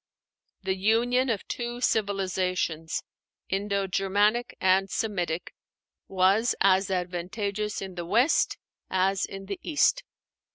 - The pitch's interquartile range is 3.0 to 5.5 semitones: No, narrow, 2.6 semitones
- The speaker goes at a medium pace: No, slow, 110 wpm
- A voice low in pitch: No, high, 195 Hz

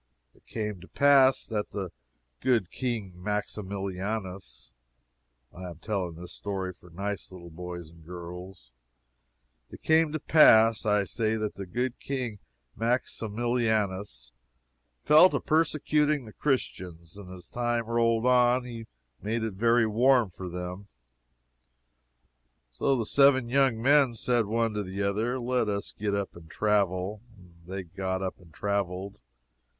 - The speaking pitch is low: Yes, low, 105 Hz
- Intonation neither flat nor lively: Yes, average, 4.4 semitones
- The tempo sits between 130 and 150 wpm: Yes, average, 140 wpm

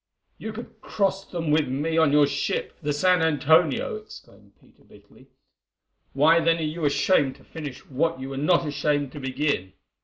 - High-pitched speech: No, medium, 150 Hz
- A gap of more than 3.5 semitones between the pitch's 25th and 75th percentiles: No, average, 3.0 semitones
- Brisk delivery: No, average, 175 wpm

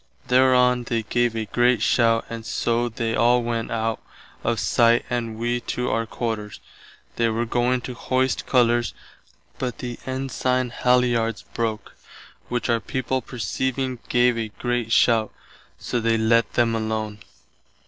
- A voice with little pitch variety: Yes, narrow, 1.5 semitones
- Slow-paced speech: No, average, 145 wpm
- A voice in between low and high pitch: No, low, 120 Hz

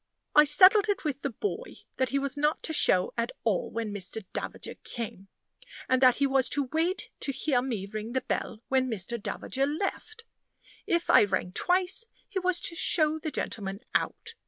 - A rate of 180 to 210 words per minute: Yes, average, 185 wpm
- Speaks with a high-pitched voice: Yes, very high, 275 Hz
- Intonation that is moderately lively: No, wide, 6.7 semitones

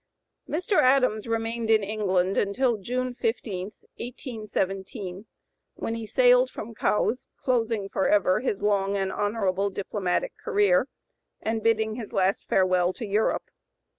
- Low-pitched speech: No, high, 215 Hz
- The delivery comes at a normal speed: No, slow, 125 wpm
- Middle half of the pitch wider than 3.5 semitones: No, average, 3.0 semitones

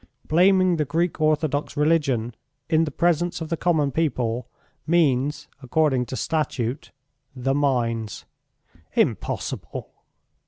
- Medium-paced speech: No, slow, 110 wpm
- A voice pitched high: No, medium, 150 Hz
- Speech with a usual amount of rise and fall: Yes, average, 4.1 semitones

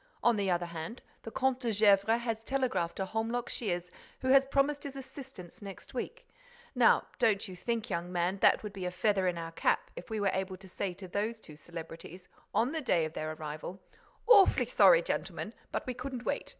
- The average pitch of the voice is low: No, high, 205 Hz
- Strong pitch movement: Yes, wide, 5.8 semitones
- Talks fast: Yes, fast, 210 wpm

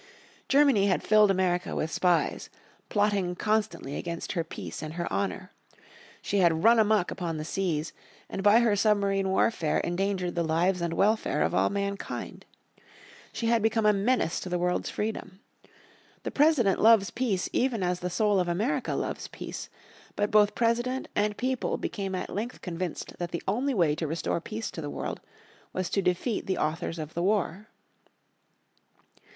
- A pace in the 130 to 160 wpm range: No, average, 170 wpm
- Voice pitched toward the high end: Yes, high, 195 Hz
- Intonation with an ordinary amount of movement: Yes, average, 3.6 semitones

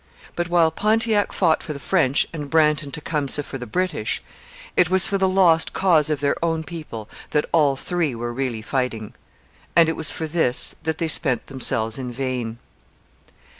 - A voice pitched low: No, medium, 155 Hz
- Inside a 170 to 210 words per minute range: Yes, average, 180 wpm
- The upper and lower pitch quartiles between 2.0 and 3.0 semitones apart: No, average, 4.4 semitones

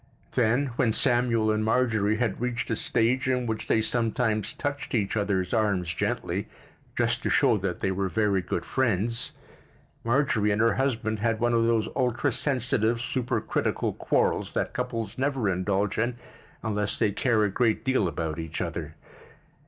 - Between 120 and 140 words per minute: No, average, 160 wpm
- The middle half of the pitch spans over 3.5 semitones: No, average, 3.1 semitones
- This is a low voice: Yes, low, 110 Hz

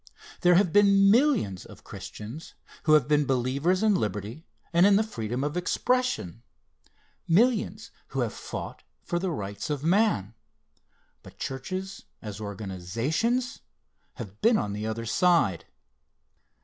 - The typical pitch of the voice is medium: Yes, medium, 155 Hz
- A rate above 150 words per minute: No, slow, 135 wpm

